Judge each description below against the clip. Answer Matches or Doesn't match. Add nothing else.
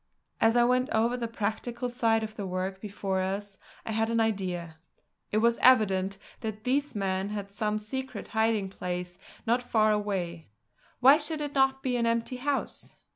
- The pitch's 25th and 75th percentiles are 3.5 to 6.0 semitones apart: Matches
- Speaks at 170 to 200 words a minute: Matches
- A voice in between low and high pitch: Doesn't match